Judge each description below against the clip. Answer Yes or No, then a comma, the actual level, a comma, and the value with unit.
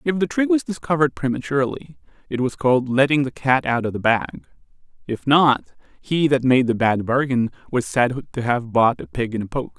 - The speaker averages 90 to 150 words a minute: No, average, 195 wpm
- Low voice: Yes, low, 125 Hz